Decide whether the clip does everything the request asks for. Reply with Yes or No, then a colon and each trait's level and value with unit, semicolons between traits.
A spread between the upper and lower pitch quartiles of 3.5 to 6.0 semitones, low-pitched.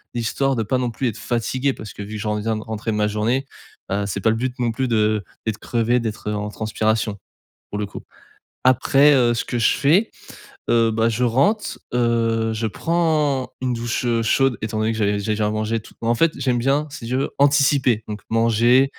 No: average, 3.0 semitones; low, 115 Hz